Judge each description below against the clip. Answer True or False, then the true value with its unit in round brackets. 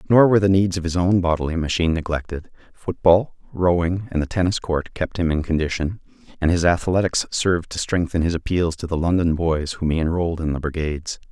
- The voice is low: True (85 Hz)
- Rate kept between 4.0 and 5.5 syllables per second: False (5.9 syllables/s)